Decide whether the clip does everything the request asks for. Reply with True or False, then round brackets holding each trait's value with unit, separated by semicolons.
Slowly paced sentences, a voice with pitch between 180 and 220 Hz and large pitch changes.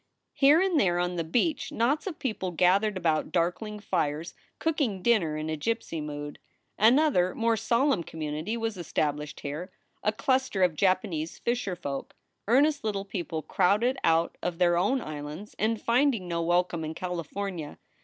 False (160 wpm; 185 Hz; 5.8 semitones)